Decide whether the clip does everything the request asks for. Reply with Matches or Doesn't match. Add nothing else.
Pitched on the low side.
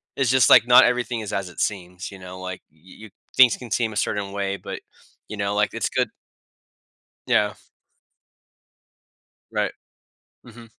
Matches